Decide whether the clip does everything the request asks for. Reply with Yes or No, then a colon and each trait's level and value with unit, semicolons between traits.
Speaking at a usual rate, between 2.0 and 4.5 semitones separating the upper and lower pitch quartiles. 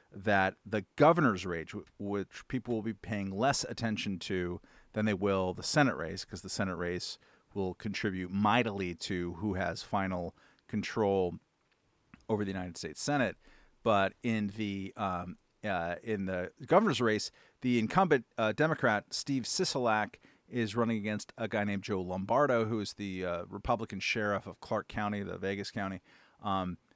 Yes: average, 160 wpm; average, 3.0 semitones